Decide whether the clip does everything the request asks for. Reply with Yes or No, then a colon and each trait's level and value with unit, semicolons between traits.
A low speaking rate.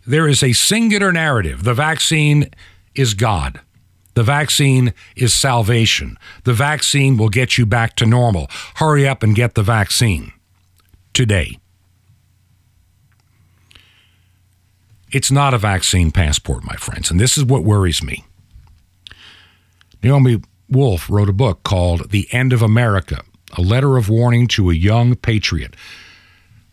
Yes: slow, 130 wpm